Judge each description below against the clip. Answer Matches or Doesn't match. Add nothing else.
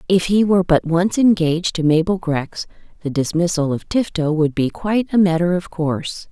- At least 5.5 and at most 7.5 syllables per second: Doesn't match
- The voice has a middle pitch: Matches